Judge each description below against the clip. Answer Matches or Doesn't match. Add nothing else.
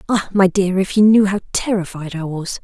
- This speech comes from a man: Doesn't match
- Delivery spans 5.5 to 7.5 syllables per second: Doesn't match